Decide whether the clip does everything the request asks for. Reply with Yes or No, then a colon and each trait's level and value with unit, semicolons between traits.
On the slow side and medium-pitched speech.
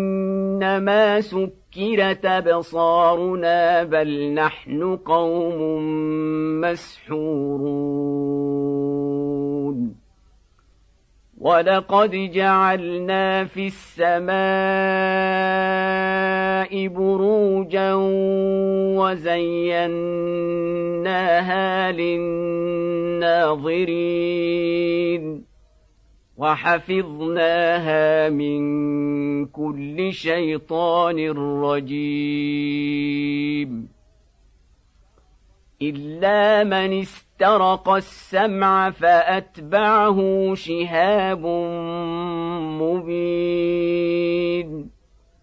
Yes: slow, 35 wpm; medium, 170 Hz